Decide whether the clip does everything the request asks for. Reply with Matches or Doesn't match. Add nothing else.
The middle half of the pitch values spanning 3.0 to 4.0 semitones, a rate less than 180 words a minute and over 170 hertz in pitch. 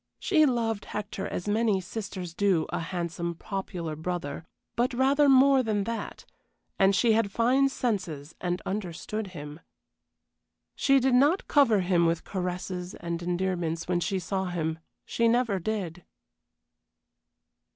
Doesn't match